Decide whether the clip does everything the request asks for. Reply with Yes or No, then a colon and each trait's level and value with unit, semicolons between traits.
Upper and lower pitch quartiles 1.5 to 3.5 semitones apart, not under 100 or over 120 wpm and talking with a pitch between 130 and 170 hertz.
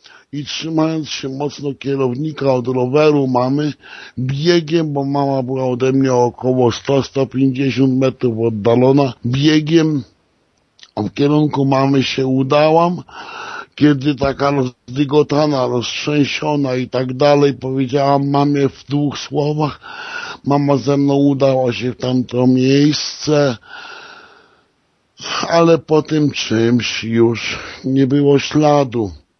Yes: average, 2.7 semitones; slow, 110 wpm; medium, 140 Hz